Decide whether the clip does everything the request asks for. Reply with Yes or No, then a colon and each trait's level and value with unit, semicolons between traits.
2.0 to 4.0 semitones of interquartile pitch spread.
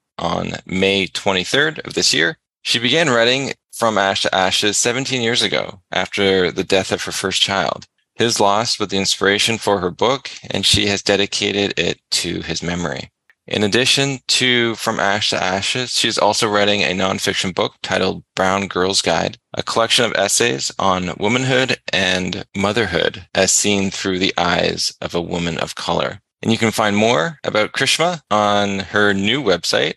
Yes: average, 3.1 semitones